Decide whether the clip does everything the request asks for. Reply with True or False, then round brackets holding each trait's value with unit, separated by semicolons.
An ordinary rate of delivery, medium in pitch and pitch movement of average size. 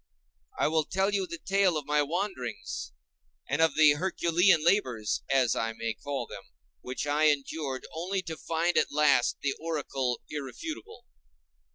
True (155 wpm; 155 Hz; 4.5 semitones)